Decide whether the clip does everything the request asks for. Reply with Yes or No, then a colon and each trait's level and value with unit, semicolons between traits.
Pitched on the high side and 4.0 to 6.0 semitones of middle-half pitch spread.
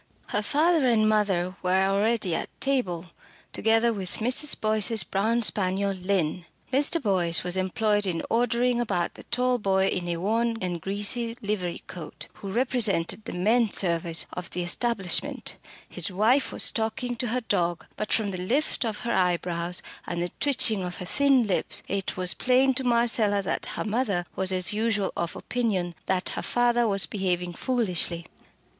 Yes: high, 205 Hz; average, 4.6 semitones